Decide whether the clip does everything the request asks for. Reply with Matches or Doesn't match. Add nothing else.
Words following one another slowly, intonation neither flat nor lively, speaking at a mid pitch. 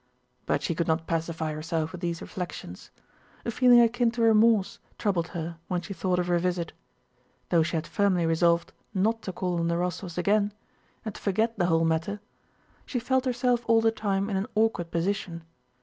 Doesn't match